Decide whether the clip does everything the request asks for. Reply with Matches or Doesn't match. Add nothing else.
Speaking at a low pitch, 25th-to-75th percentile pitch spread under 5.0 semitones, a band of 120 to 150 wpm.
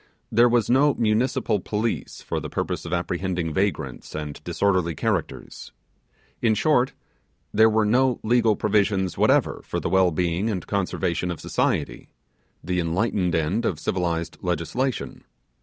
Matches